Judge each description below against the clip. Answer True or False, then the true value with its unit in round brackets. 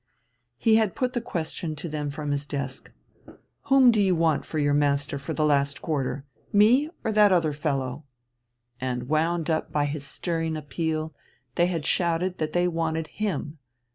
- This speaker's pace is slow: False (170 wpm)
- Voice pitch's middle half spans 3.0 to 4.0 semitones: True (3.5 semitones)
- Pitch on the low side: False (155 Hz)